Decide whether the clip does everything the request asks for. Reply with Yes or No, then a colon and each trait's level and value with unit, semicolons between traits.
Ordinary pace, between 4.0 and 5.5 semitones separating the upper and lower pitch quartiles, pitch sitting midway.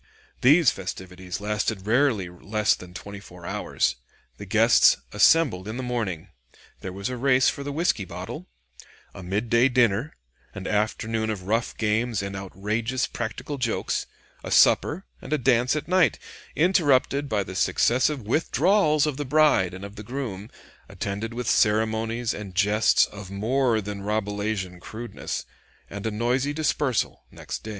No: average, 150 wpm; average, 4.6 semitones; low, 110 Hz